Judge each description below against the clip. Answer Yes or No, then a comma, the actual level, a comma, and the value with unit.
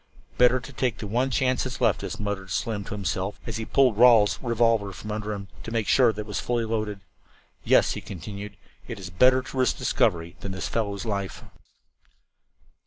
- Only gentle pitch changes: No, average, 3.3 semitones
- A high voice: No, low, 105 Hz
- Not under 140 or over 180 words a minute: No, average, 190 wpm